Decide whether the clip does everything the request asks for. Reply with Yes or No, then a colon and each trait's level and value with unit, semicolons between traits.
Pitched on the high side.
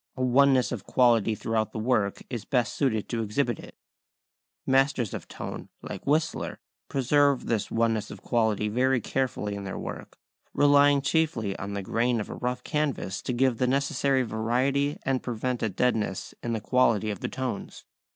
No: low, 125 Hz